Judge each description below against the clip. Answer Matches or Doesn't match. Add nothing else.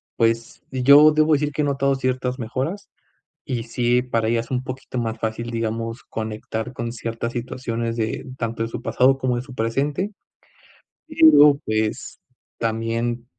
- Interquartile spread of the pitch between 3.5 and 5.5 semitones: Doesn't match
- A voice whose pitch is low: Matches